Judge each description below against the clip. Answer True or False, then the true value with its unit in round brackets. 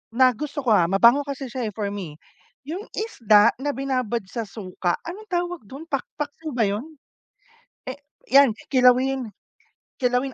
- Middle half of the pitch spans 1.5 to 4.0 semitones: False (4.6 semitones)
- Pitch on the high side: True (255 Hz)